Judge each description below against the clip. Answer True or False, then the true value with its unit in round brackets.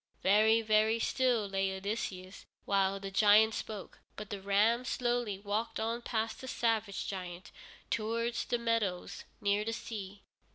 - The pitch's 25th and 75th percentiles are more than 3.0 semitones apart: False (2.6 semitones)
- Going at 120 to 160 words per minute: True (140 wpm)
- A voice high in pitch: True (215 Hz)